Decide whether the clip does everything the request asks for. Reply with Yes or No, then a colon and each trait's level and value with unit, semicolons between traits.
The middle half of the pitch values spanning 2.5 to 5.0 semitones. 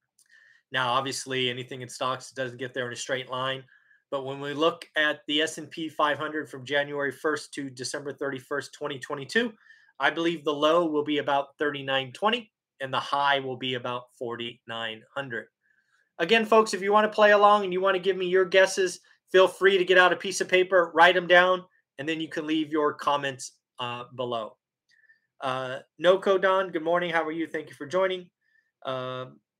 No: wide, 5.6 semitones